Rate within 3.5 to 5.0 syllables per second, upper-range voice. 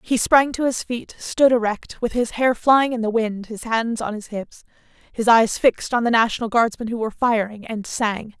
Yes: 4.9 syllables/s; high, 230 Hz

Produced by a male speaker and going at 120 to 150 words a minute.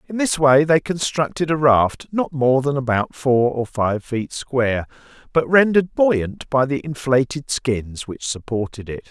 No: male; average, 170 wpm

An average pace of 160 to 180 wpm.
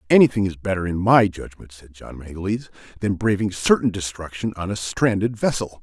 Yes: average, 175 wpm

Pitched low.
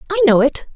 No: very high, 315 Hz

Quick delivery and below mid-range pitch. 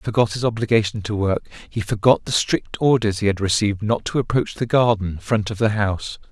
Yes: fast, 220 wpm; low, 105 Hz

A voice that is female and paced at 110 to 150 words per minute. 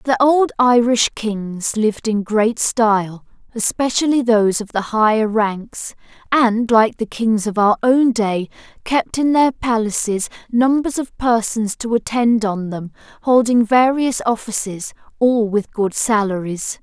Yes: female; slow, 135 wpm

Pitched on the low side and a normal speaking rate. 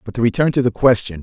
No: low, 115 Hz; fast, 295 wpm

